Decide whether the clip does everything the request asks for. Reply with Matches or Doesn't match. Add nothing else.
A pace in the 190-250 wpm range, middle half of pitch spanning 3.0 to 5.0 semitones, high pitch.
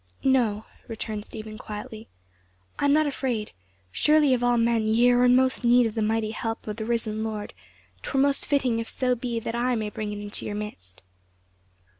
Doesn't match